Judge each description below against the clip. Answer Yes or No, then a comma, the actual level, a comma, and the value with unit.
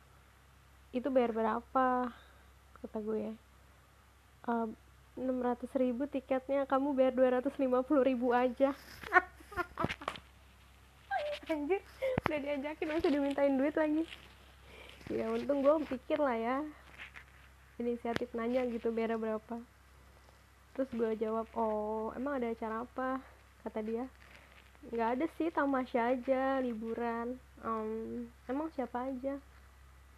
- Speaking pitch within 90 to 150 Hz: No, very high, 255 Hz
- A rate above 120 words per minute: No, average, 105 wpm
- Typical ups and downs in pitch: Yes, average, 3.5 semitones